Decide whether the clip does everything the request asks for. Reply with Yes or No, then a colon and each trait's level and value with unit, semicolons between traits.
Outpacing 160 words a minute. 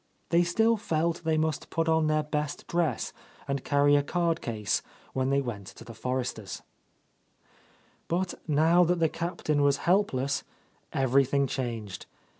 No: average, 150 wpm